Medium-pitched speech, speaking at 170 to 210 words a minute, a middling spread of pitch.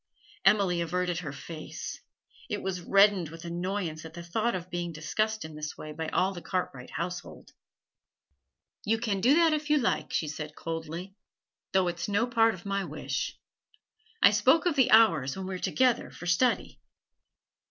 Yes: medium, 180 Hz; average, 175 wpm; average, 4.5 semitones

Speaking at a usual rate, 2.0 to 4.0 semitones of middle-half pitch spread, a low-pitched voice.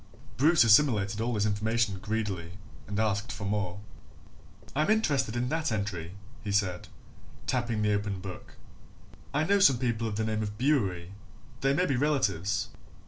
No: average, 155 wpm; average, 4.5 semitones; low, 110 Hz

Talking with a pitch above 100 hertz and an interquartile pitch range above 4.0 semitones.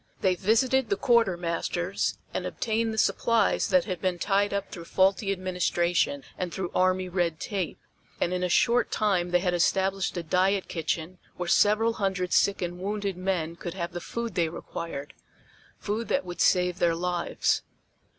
No: medium, 185 Hz; narrow, 2.6 semitones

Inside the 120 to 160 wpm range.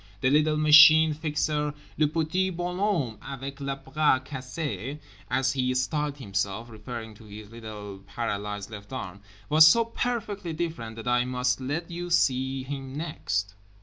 Yes: average, 150 wpm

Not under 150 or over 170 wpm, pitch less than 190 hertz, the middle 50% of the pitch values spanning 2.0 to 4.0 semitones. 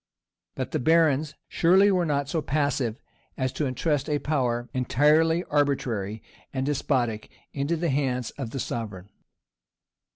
No: slow, 135 wpm; medium, 140 Hz; average, 3.7 semitones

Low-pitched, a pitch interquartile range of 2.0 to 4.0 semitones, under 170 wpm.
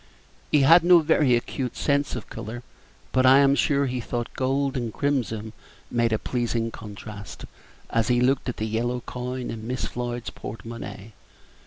No: low, 125 Hz; average, 2.8 semitones; average, 175 wpm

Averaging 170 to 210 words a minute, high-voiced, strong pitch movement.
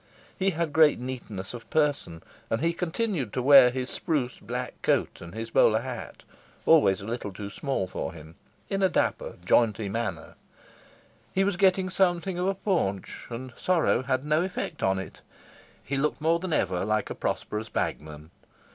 No: average, 175 wpm; low, 130 Hz; wide, 8.0 semitones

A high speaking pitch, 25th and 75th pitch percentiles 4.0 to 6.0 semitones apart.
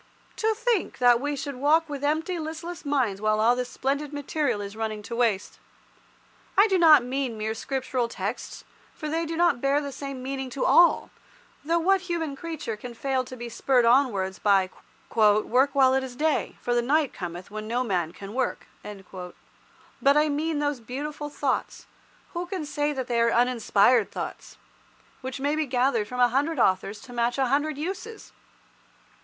Yes: very high, 265 Hz; average, 4.3 semitones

